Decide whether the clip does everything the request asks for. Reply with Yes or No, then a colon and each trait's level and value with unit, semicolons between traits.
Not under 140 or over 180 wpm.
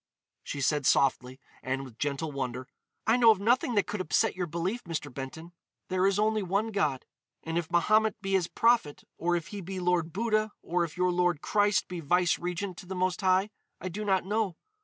No: fast, 205 wpm